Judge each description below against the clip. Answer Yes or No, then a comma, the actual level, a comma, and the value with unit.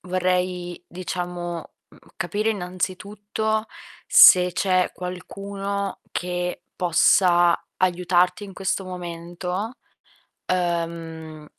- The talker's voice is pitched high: No, medium, 180 Hz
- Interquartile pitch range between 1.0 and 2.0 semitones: Yes, narrow, 1.7 semitones